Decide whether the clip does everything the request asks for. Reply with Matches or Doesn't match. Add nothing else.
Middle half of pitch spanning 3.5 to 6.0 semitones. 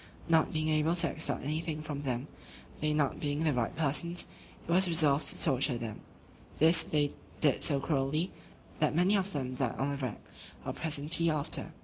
Doesn't match